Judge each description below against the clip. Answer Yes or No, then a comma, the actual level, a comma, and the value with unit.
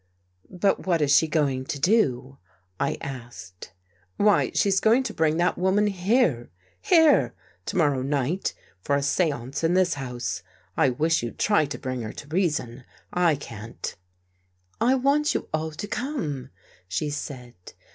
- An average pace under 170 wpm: No, average, 175 wpm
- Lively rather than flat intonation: Yes, wide, 7.2 semitones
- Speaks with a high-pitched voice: No, medium, 145 Hz